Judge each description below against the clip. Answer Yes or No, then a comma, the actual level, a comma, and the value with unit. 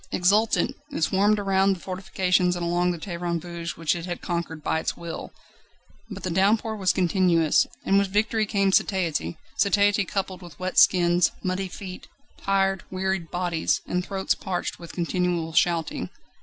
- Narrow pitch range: Yes, narrow, 2.2 semitones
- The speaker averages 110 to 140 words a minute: No, average, 160 wpm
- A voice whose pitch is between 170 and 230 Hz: Yes, medium, 185 Hz